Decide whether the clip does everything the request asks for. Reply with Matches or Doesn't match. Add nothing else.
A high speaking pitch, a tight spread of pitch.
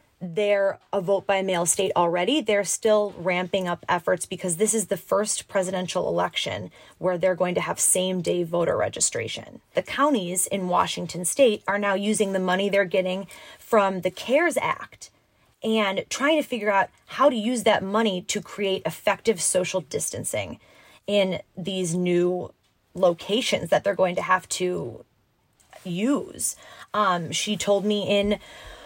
Matches